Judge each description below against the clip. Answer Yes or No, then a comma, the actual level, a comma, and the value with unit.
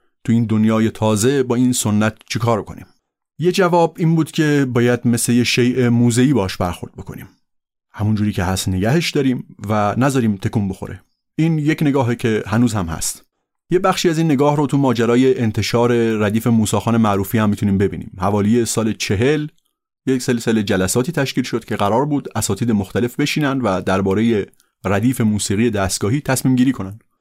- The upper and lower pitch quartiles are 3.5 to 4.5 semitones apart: Yes, average, 4.0 semitones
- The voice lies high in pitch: No, low, 120 Hz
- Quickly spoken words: Yes, fast, 170 wpm